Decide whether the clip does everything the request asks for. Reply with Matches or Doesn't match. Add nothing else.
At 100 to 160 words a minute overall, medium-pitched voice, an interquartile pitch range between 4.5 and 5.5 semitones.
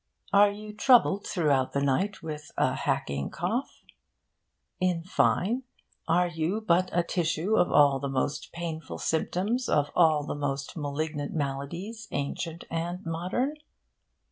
Matches